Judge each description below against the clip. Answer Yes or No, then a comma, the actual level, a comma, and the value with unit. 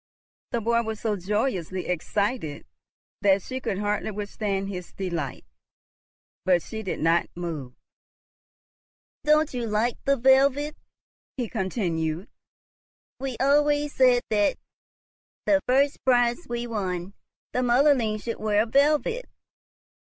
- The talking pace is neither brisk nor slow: No, slow, 115 wpm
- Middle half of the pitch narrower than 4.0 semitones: No, wide, 5.4 semitones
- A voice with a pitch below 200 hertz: No, high, 220 Hz